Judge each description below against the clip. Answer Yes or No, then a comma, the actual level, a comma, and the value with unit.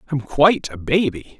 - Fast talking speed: No, average, 170 wpm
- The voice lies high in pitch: No, medium, 140 Hz